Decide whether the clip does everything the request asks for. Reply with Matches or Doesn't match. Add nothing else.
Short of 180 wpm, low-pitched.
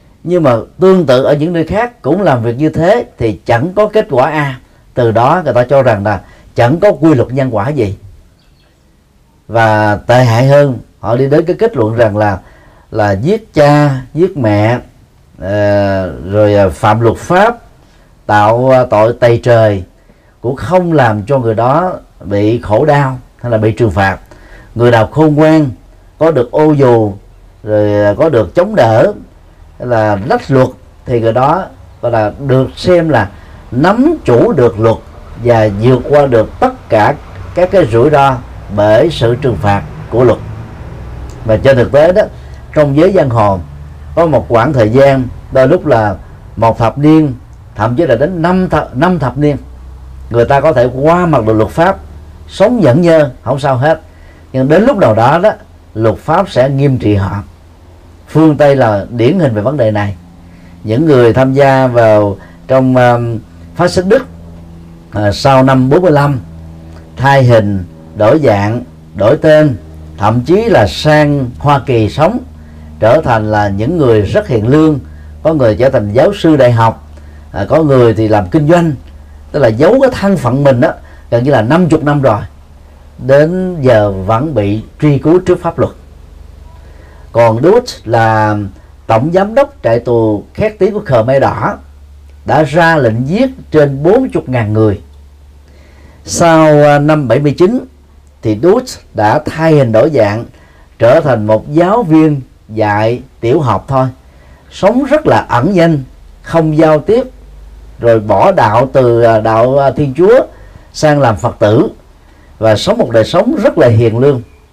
Matches